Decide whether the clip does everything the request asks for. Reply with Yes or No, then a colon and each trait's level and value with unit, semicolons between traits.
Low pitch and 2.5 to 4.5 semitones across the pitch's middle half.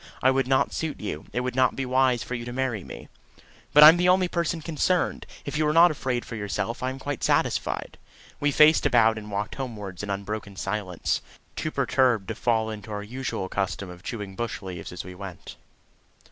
No: low, 120 Hz; average, 5.0 semitones